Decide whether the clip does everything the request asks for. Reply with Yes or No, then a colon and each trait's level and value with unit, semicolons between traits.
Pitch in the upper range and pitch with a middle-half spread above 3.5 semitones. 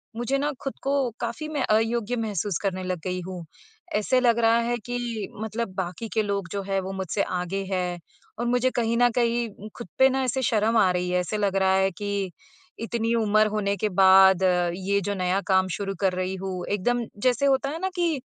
Yes: high, 205 Hz; average, 4.0 semitones